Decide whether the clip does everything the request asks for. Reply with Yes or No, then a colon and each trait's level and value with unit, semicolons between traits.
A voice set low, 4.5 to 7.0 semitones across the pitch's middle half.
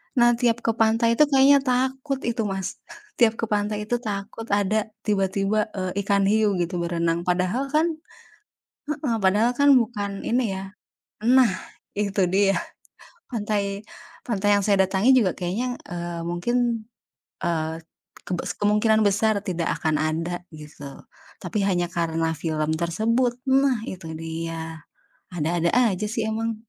No: high, 205 Hz; average, 4.8 semitones